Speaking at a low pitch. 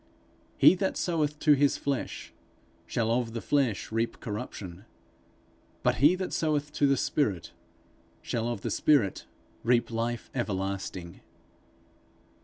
Yes: low, 120 Hz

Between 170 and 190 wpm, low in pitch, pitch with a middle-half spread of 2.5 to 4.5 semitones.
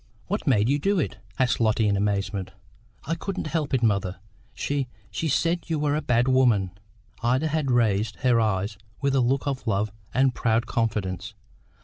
No: average, 175 wpm; low, 120 Hz; average, 5.2 semitones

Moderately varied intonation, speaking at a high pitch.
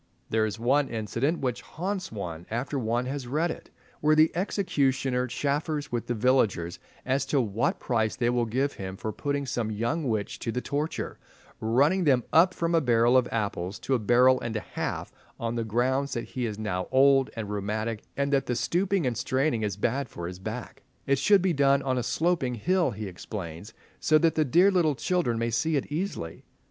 No: average, 4.7 semitones; low, 125 Hz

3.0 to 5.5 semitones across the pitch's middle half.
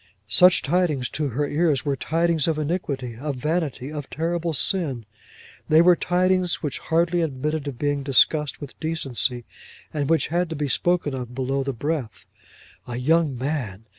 Yes: average, 3.8 semitones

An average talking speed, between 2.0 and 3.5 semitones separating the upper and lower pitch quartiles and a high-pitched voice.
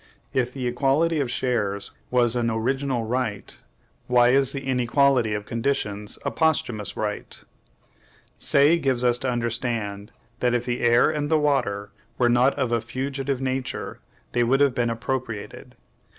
No: average, 150 wpm; average, 2.7 semitones; low, 125 Hz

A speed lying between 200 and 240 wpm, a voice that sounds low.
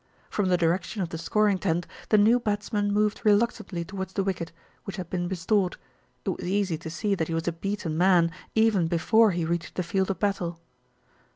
No: fast, 205 wpm; high, 190 Hz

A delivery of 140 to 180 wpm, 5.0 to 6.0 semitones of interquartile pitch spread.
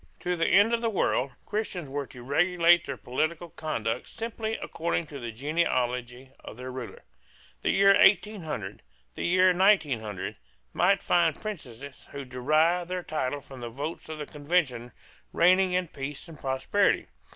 Yes: average, 155 wpm; wide, 5.6 semitones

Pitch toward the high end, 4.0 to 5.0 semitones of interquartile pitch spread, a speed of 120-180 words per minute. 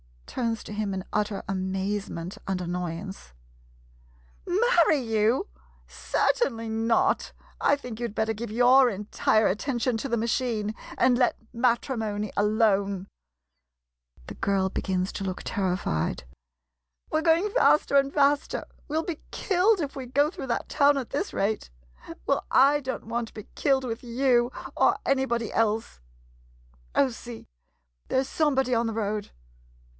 Yes: high, 230 Hz; average, 4.7 semitones; average, 150 wpm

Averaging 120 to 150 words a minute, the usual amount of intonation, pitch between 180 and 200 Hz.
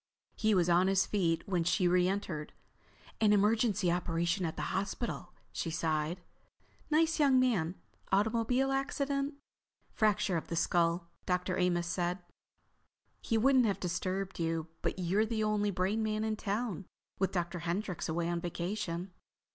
Yes: average, 140 wpm; average, 3.9 semitones; high, 190 Hz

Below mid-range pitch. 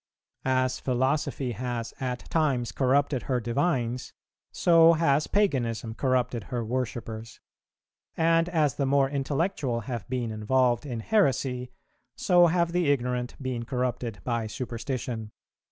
Yes: low, 130 Hz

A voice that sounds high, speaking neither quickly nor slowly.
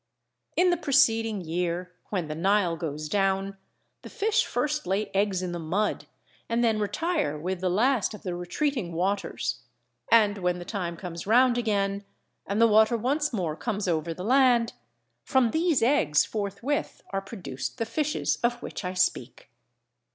Yes: high, 200 Hz; average, 165 wpm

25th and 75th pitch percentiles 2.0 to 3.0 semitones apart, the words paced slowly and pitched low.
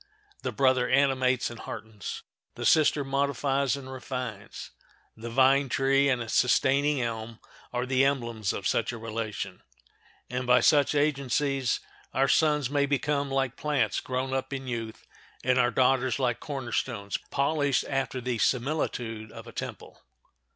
No: narrow, 2.5 semitones; average, 150 wpm; low, 130 Hz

